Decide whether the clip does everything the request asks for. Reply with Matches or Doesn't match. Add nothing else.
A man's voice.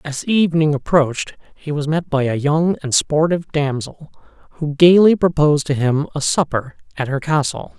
Matches